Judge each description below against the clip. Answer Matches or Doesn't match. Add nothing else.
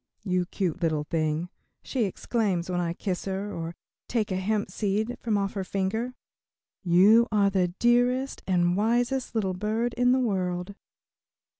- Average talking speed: Matches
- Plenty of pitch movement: Doesn't match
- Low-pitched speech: Doesn't match